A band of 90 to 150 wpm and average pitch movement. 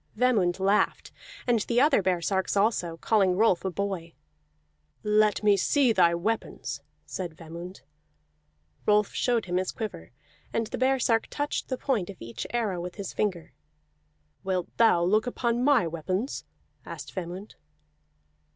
Yes: average, 140 wpm; average, 4.2 semitones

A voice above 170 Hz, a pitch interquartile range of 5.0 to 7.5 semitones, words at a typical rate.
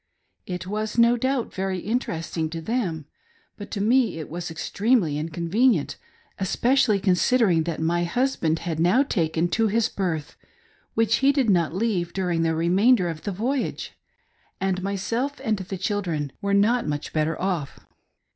Yes: high, 190 Hz; wide, 5.4 semitones; average, 160 wpm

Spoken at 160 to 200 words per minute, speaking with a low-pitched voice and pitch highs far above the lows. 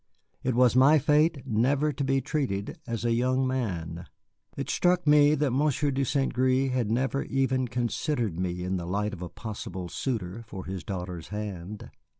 Yes: average, 175 wpm; low, 125 Hz; wide, 5.7 semitones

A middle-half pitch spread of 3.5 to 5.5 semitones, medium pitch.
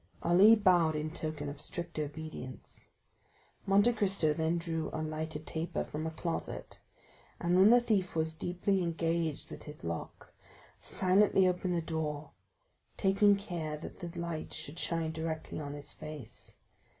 No: average, 2.9 semitones; medium, 165 Hz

